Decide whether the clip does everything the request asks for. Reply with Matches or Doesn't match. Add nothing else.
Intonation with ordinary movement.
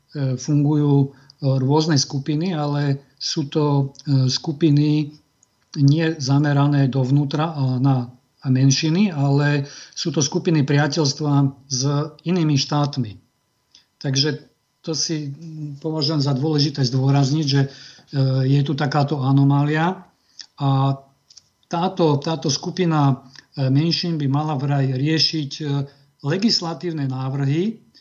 Doesn't match